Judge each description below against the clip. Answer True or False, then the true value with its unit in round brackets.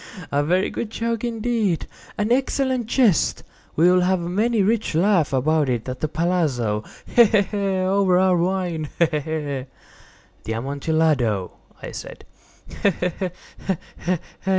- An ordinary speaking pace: False (125 wpm)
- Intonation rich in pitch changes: True (5.8 semitones)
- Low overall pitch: False (180 Hz)